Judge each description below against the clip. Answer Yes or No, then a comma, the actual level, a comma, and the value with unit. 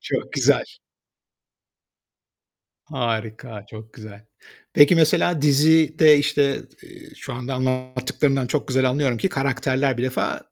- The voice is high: No, low, 130 Hz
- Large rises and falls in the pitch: No, average, 2.8 semitones